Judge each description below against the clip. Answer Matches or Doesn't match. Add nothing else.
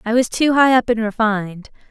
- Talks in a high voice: Matches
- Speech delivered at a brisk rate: Matches